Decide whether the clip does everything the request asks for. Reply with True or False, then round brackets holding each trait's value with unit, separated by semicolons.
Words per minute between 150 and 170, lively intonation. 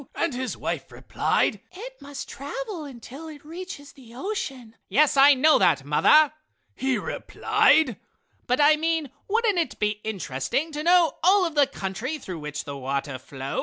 True (165 wpm; 6.9 semitones)